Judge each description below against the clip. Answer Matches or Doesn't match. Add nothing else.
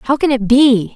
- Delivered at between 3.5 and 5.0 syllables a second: Matches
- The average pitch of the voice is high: Matches